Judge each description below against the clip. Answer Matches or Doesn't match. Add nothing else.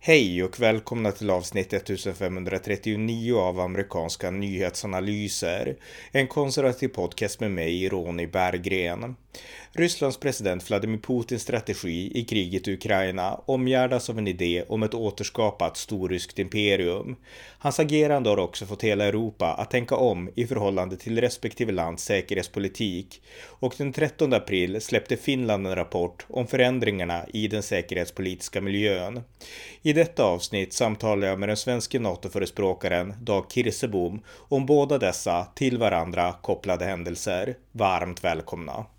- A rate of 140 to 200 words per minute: Doesn't match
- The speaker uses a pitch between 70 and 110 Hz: Matches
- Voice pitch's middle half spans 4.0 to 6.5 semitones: Matches